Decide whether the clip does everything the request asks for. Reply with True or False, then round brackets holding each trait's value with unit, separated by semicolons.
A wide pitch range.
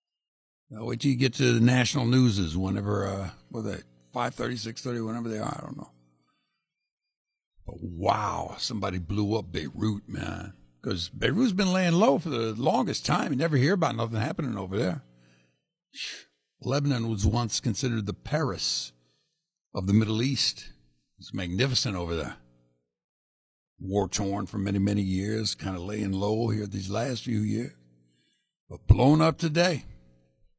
True (6.2 semitones)